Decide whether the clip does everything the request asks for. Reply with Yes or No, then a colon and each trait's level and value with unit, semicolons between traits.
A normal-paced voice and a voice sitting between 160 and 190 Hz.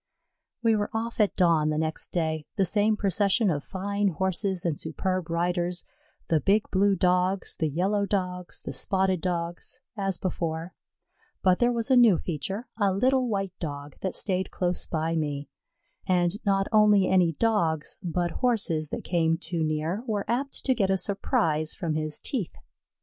Yes: average, 165 wpm; medium, 185 Hz